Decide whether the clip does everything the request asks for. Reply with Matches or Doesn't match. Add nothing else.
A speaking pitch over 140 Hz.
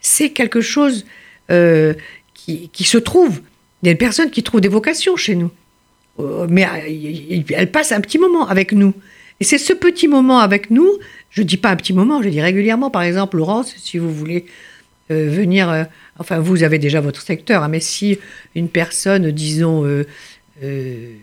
Matches